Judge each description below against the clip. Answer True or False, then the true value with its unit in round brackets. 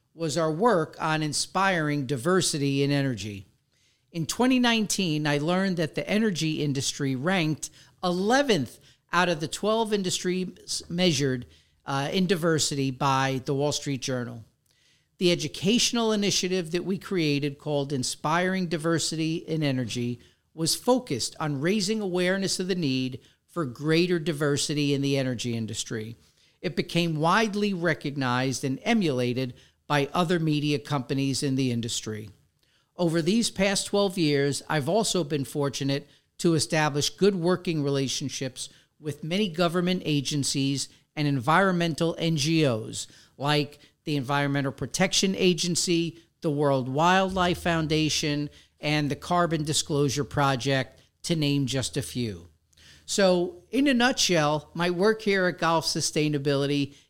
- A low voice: False (155 Hz)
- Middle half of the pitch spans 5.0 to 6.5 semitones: False (4.4 semitones)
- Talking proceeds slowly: True (125 wpm)